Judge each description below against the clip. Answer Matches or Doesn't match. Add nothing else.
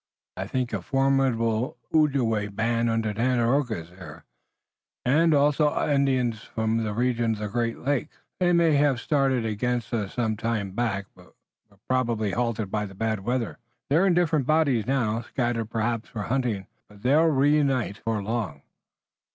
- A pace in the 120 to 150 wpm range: Doesn't match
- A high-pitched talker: Doesn't match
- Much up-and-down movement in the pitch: Doesn't match